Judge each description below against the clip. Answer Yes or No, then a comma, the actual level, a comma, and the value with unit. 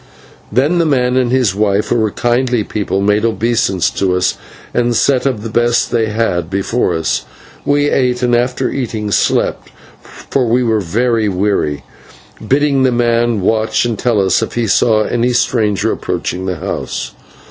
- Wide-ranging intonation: No, average, 3.2 semitones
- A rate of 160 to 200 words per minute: Yes, average, 170 wpm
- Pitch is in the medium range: No, low, 115 Hz